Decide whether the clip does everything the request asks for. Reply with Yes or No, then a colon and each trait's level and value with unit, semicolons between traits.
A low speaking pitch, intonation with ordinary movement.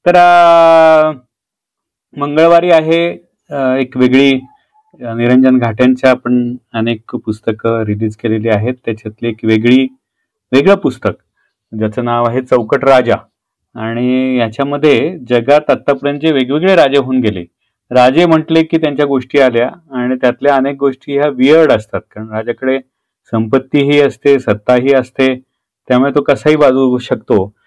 Yes: low, 130 Hz; average, 3.4 semitones